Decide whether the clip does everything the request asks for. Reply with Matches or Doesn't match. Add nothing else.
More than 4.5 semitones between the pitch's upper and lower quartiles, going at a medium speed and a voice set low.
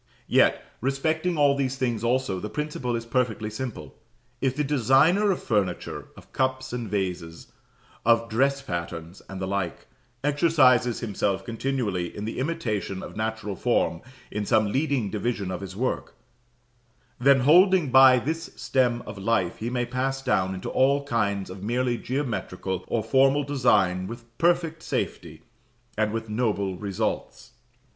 Matches